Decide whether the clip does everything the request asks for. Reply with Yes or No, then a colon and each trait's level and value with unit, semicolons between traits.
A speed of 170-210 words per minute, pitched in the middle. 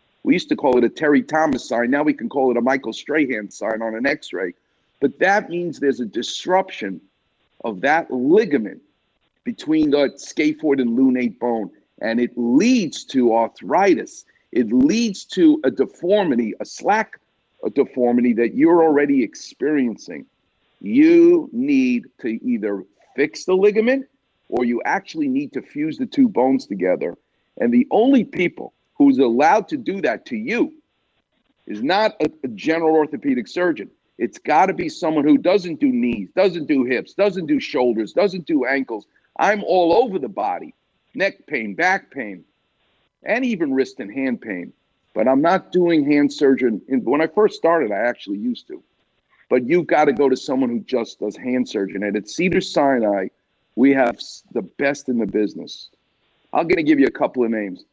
Yes: average, 175 wpm; medium, 175 Hz